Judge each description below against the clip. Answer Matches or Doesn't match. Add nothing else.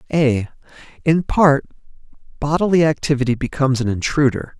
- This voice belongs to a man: Matches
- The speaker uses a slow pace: Matches